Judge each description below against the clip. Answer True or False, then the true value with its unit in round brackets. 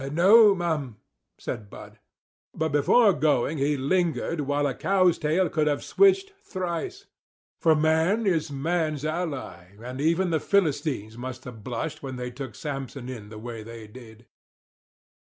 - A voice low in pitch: False (150 Hz)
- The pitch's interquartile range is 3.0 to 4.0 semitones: False (5.4 semitones)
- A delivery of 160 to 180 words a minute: False (150 wpm)